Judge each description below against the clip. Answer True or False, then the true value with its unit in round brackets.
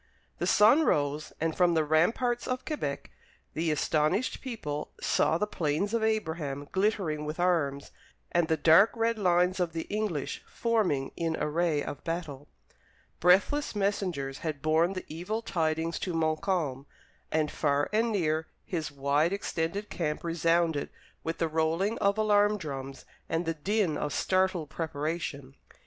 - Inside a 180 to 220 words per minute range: False (145 wpm)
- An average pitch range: True (4.7 semitones)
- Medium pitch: True (165 Hz)